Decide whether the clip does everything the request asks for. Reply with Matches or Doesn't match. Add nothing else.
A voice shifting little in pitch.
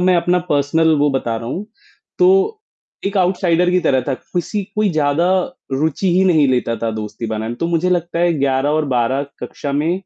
Doesn't match